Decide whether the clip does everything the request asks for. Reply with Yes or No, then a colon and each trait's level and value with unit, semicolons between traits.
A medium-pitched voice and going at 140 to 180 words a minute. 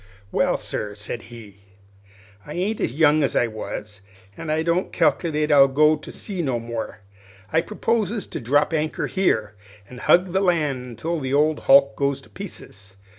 Yes: medium, 150 Hz; average, 175 wpm